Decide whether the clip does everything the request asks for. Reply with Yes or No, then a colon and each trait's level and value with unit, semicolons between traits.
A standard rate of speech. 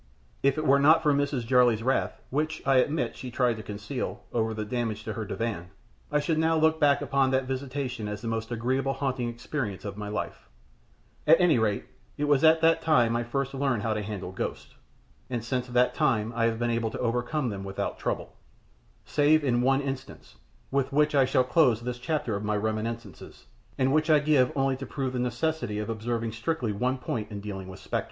No: fast, 210 wpm